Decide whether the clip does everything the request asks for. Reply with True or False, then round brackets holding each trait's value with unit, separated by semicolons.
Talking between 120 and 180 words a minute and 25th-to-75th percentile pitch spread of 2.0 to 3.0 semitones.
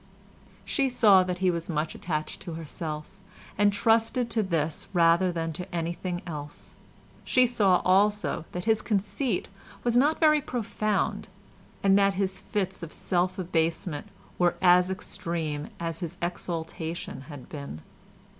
False (140 wpm; 3.8 semitones)